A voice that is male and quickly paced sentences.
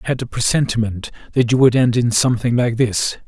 Yes: male; fast, 220 wpm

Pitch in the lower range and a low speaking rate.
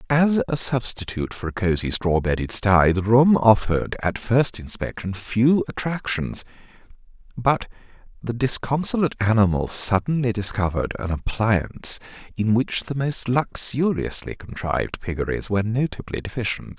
Yes: low, 115 Hz; slow, 125 wpm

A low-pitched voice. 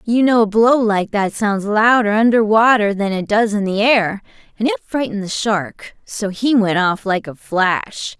No: high, 215 Hz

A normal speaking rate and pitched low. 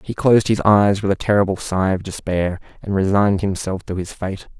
No: fast, 210 wpm; low, 100 Hz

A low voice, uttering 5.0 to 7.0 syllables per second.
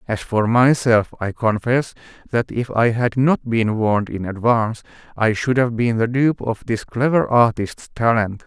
No: low, 115 Hz; 4.4 syllables/s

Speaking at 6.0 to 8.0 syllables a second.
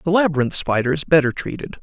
Yes: 6.5 syllables/s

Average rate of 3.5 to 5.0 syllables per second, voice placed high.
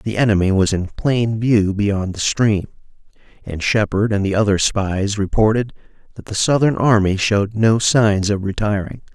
No: 4.6 syllables/s; low, 105 Hz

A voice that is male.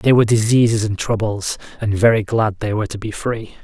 Yes: male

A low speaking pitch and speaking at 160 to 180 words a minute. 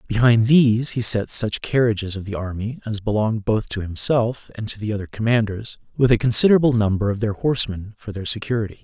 No: low, 110 Hz; average, 195 wpm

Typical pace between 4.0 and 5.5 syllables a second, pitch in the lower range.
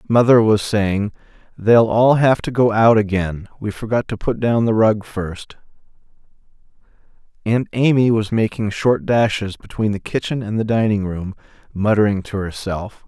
Yes: 4.6 syllables/s; low, 105 Hz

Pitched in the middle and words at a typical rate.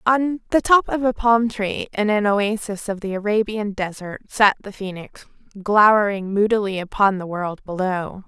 No: high, 205 Hz; average, 165 wpm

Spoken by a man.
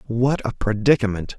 Yes: male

